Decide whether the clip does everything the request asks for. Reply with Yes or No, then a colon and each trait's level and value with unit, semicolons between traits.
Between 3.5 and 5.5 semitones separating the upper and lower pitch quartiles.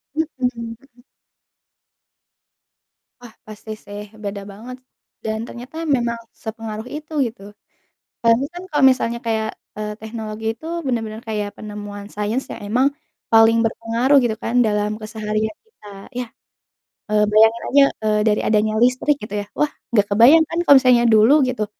No: narrow, 2.6 semitones